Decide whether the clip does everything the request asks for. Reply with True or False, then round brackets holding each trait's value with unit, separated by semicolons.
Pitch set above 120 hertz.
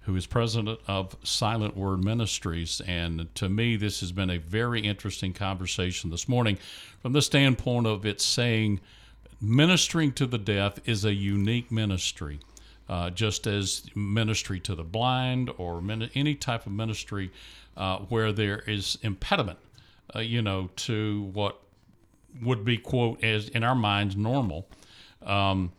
False (105 Hz)